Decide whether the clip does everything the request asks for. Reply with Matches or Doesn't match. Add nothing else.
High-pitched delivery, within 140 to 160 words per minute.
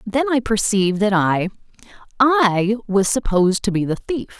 Matches